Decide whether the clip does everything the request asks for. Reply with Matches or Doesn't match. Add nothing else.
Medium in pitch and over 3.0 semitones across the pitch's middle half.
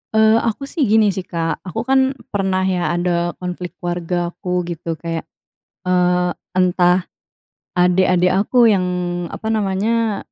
Matches